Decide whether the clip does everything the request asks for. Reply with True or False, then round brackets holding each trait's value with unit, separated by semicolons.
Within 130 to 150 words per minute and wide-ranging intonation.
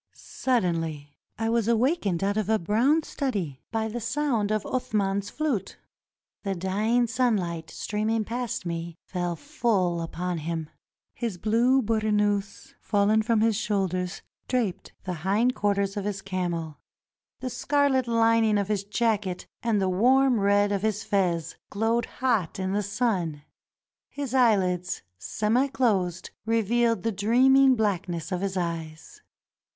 False (135 wpm; 4.1 semitones)